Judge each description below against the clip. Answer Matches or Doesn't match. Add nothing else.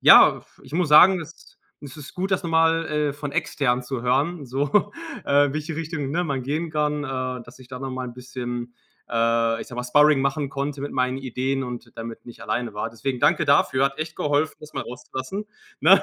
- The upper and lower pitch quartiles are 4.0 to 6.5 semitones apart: Doesn't match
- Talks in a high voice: Doesn't match